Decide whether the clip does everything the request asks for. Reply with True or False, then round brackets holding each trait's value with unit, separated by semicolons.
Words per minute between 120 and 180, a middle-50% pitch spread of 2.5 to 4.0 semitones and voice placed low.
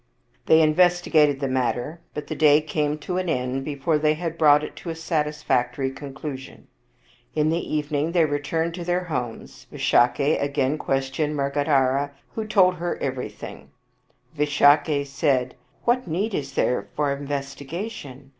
False (155 wpm; 2.8 semitones; 150 Hz)